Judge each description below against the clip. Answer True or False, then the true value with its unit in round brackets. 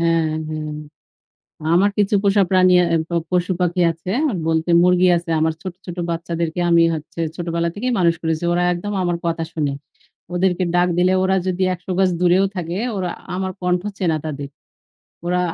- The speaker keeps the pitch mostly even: True (1.8 semitones)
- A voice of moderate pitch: True (175 Hz)